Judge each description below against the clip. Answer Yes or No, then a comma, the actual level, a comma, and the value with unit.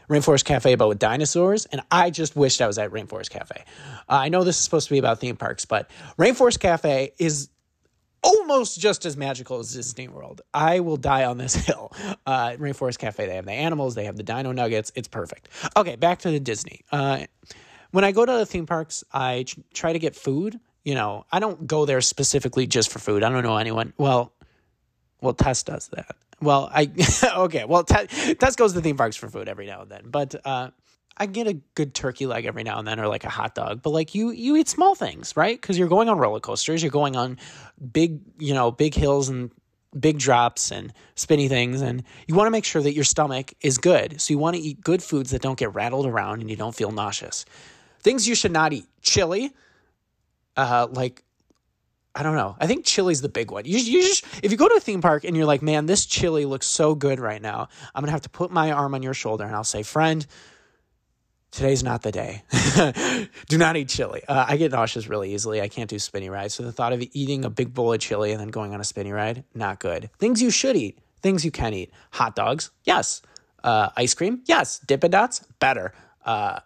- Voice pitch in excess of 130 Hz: Yes, medium, 140 Hz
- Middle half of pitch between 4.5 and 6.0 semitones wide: Yes, wide, 5.4 semitones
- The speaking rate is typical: No, fast, 225 wpm